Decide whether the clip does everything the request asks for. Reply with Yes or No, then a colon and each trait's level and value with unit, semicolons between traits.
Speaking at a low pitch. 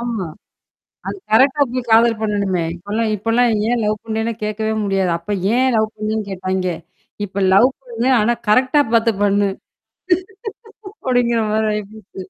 No: high, 220 Hz